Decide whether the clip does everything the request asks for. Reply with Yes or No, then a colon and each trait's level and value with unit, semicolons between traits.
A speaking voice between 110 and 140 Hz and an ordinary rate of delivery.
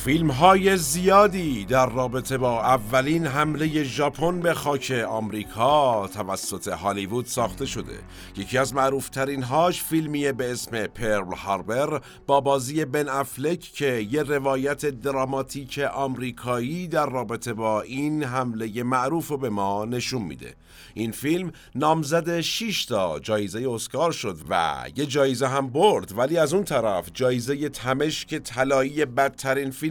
Yes: low, 135 Hz; average, 135 wpm